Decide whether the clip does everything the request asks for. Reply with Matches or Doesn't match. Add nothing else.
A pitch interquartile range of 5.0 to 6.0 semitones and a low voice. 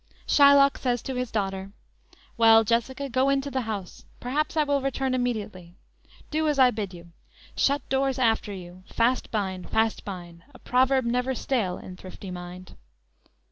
Doesn't match